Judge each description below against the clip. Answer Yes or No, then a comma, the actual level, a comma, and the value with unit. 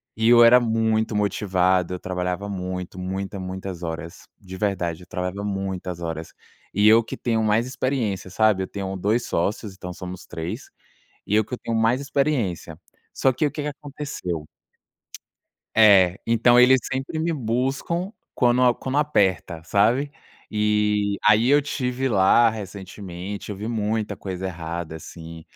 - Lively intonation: No, average, 4.5 semitones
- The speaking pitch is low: Yes, low, 105 Hz